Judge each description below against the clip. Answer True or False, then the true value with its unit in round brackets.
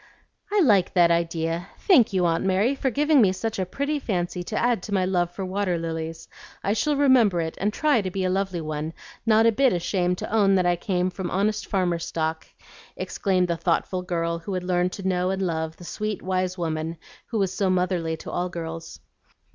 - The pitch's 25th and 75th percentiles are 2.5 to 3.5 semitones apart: True (3.1 semitones)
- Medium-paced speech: False (210 wpm)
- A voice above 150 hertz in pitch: True (185 Hz)